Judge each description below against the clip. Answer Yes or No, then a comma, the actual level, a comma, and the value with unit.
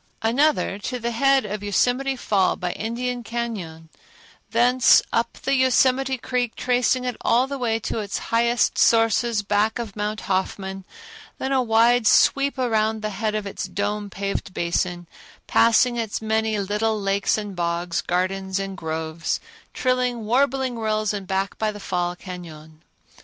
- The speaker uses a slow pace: No, average, 150 wpm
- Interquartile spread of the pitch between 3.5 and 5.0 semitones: Yes, average, 3.9 semitones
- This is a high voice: Yes, high, 220 Hz